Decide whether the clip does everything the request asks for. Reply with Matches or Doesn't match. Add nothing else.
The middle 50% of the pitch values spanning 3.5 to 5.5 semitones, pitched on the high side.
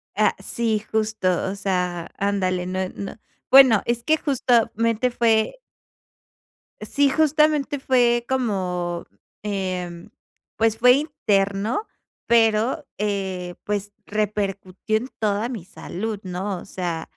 Matches